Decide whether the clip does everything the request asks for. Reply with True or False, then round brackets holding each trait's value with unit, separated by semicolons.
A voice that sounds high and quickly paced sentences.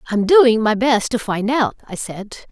True (230 Hz; 215 wpm)